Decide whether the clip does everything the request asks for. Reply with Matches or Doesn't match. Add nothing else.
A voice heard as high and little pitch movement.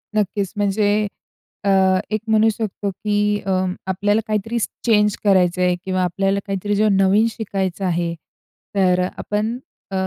Matches